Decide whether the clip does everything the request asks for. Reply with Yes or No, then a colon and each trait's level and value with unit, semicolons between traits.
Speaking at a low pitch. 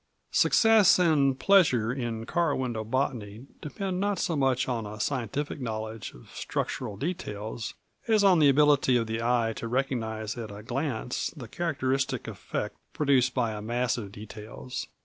Yes: low, 125 Hz